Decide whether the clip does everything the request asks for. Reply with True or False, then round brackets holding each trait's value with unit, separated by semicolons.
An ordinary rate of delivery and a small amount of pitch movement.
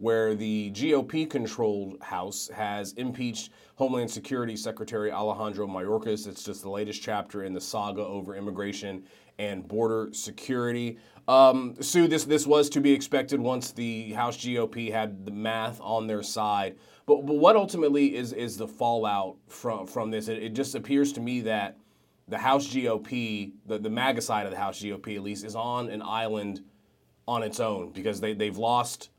False (175 wpm; 3.1 semitones)